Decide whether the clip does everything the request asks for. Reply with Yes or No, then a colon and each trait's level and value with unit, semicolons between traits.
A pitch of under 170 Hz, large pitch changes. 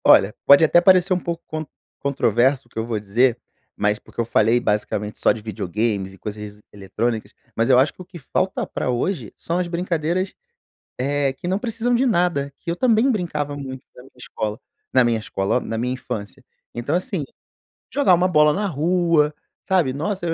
Yes: medium, 140 Hz; wide, 7.4 semitones